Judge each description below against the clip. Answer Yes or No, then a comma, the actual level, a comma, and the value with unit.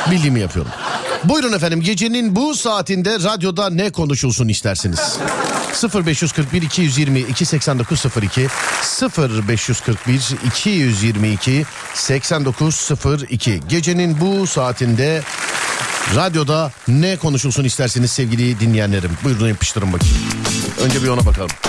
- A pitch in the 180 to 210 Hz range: No, low, 135 Hz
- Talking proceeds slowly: Yes, slow, 90 wpm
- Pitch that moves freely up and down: Yes, wide, 6.3 semitones